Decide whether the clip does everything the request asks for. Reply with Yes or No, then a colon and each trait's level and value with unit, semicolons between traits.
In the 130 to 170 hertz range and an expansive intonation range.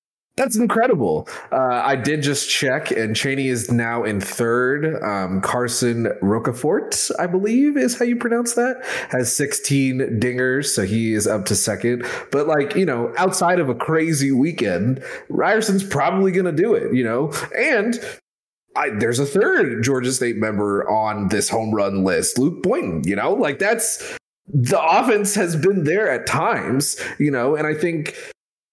Yes: low, 135 Hz; wide, 7.8 semitones